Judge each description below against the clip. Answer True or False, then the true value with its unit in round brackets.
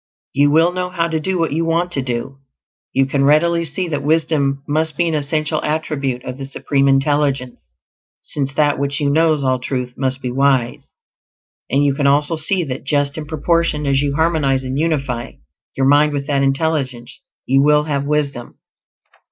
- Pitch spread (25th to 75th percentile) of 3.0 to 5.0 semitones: False (2.4 semitones)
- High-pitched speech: False (145 Hz)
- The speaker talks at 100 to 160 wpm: False (180 wpm)